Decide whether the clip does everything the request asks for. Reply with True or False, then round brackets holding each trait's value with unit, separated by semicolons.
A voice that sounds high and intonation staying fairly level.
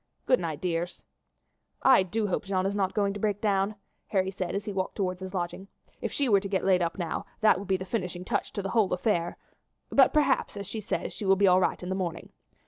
True (195 Hz; 2.0 semitones)